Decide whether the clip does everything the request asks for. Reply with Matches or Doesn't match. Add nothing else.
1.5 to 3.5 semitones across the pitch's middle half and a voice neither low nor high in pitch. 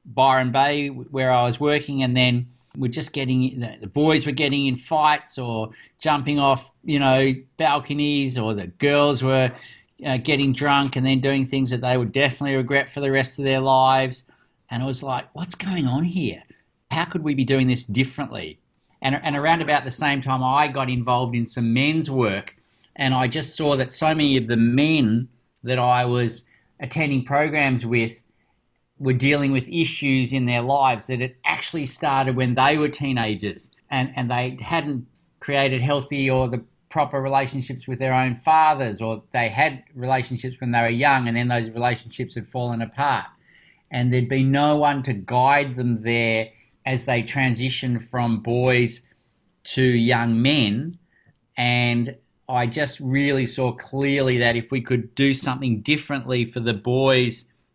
Doesn't match